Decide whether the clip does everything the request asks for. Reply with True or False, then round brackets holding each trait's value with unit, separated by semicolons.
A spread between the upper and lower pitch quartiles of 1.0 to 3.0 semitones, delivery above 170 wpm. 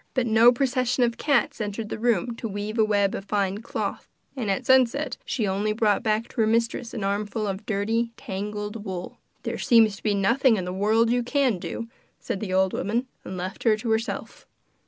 True (2.7 semitones; 200 wpm)